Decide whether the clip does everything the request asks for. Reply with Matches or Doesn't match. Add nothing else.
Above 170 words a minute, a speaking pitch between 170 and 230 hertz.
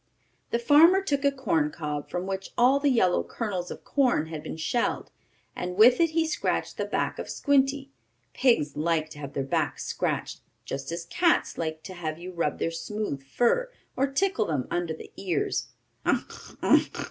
Matches